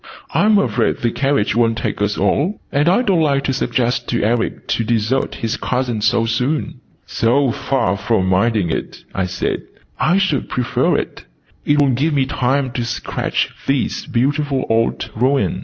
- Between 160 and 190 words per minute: Yes, average, 170 wpm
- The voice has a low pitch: Yes, low, 125 Hz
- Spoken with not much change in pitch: No, average, 3.7 semitones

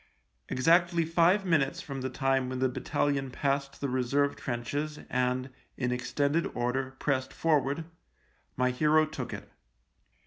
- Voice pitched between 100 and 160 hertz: Yes, low, 135 Hz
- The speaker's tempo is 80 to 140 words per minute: Yes, slow, 135 wpm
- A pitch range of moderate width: Yes, average, 3.1 semitones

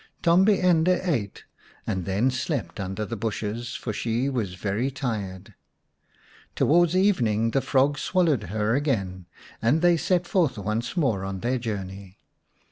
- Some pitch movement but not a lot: No, wide, 7.4 semitones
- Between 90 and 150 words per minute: Yes, average, 145 wpm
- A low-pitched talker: Yes, low, 120 Hz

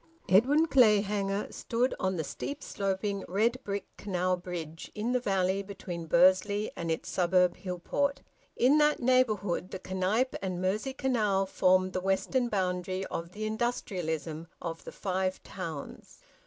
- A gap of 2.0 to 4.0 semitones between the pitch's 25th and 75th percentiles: Yes, average, 3.2 semitones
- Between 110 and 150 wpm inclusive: Yes, average, 140 wpm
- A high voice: Yes, high, 195 Hz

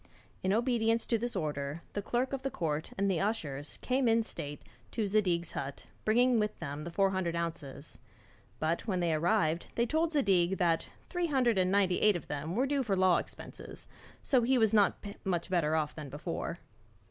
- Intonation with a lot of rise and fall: Yes, wide, 5.7 semitones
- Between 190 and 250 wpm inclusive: Yes, average, 195 wpm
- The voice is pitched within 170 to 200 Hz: Yes, high, 190 Hz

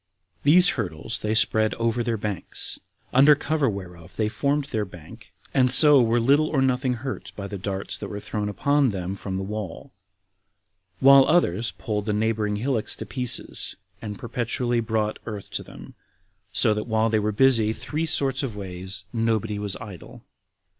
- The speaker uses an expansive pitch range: No, average, 4.1 semitones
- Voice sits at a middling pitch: No, low, 110 Hz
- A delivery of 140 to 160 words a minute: No, average, 170 wpm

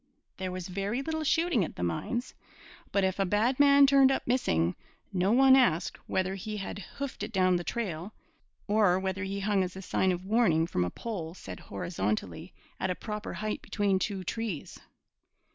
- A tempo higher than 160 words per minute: Yes, average, 185 wpm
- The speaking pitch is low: No, high, 195 Hz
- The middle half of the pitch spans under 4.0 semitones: No, average, 4.3 semitones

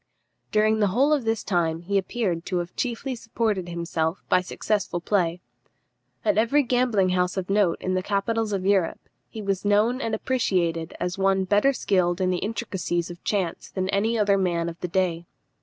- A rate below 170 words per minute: No, average, 185 wpm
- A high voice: Yes, high, 195 Hz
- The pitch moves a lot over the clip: No, average, 3.7 semitones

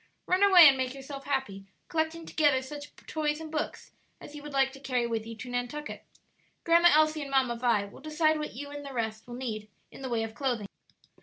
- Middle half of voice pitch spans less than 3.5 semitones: No, average, 4.1 semitones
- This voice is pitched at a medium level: No, very high, 270 Hz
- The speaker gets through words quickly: Yes, fast, 220 wpm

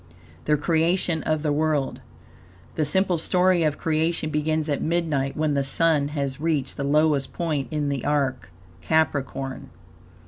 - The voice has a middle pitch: Yes, medium, 150 Hz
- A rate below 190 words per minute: Yes, average, 145 wpm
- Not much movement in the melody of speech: Yes, narrow, 2.2 semitones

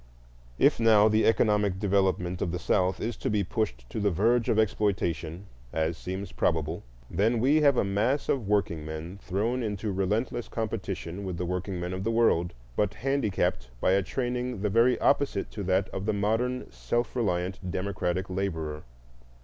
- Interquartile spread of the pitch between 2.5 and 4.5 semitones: Yes, average, 3.7 semitones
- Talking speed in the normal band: Yes, average, 165 wpm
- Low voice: Yes, low, 100 Hz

